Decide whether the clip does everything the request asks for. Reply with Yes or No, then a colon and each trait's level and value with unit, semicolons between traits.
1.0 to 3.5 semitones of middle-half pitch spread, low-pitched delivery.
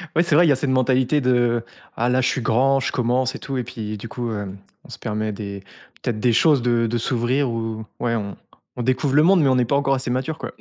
Yes: average, 2.7 semitones; low, 125 Hz